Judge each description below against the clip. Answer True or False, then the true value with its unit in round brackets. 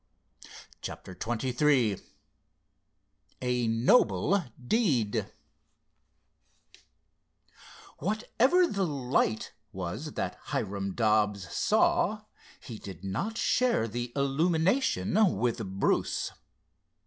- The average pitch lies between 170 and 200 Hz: False (120 Hz)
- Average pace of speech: False (75 wpm)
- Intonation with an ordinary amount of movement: False (8.9 semitones)